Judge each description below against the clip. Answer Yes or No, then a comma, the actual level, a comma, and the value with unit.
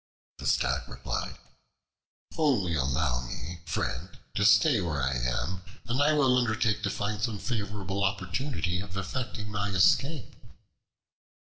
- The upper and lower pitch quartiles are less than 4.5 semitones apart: No, average, 5.2 semitones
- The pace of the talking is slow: Yes, slow, 130 wpm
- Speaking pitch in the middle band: No, low, 100 Hz